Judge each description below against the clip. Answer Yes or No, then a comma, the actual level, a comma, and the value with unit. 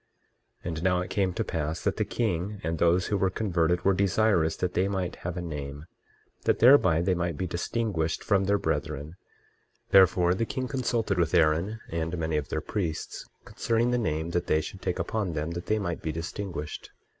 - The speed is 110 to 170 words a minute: No, average, 200 wpm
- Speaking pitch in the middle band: No, very low, 90 Hz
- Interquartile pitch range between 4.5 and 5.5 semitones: No, average, 3.6 semitones